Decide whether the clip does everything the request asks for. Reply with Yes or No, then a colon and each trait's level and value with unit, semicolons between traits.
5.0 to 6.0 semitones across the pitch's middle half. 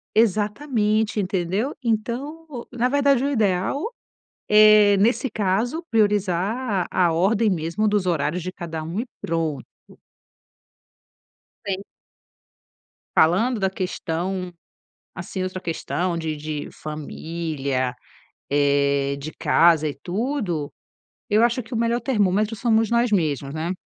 Yes: wide, 5.4 semitones